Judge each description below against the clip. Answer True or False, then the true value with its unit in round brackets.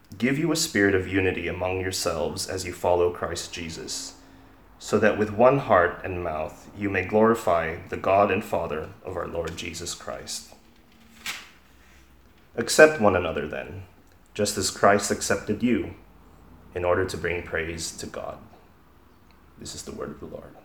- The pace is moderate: True (160 wpm)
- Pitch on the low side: True (95 Hz)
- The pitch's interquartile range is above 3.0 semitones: True (3.6 semitones)